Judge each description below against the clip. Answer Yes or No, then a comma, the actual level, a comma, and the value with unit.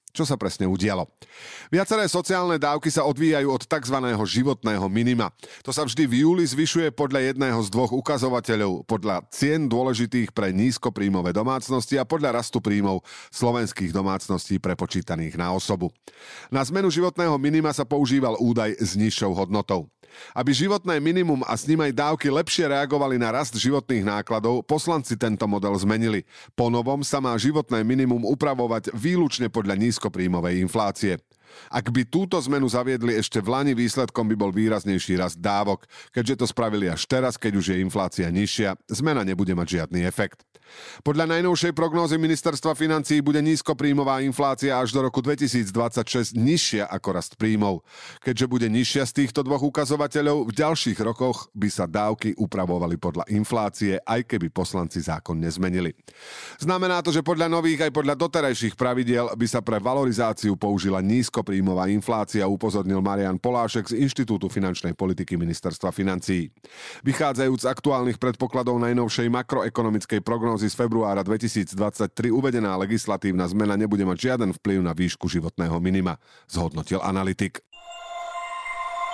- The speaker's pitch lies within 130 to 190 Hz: No, low, 120 Hz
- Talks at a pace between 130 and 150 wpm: Yes, average, 145 wpm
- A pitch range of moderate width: No, wide, 6.0 semitones